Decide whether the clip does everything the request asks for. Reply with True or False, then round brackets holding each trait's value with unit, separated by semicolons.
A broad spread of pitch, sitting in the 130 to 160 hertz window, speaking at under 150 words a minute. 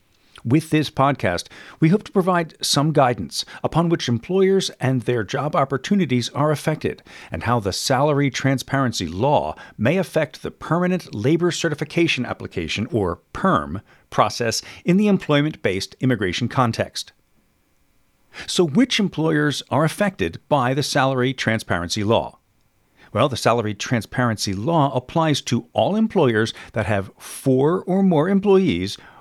True (6.4 semitones; 135 Hz; 135 wpm)